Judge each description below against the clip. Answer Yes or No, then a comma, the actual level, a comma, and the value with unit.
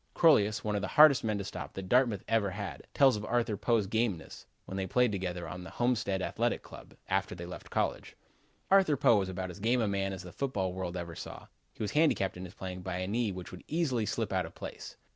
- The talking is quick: Yes, fast, 245 wpm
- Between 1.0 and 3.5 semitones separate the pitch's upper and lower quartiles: No, average, 4.2 semitones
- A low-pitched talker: Yes, low, 100 Hz